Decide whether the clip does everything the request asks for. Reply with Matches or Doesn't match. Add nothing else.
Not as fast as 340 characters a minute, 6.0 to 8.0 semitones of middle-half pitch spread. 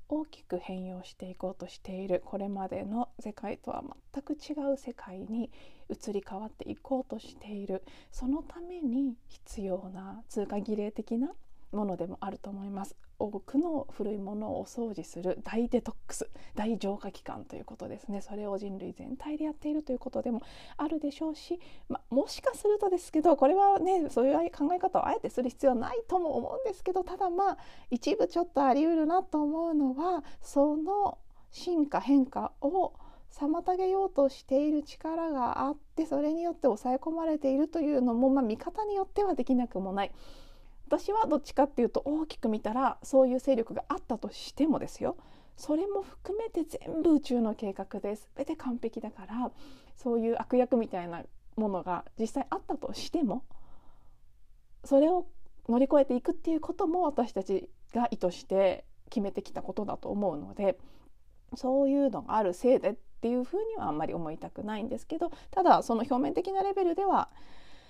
Doesn't match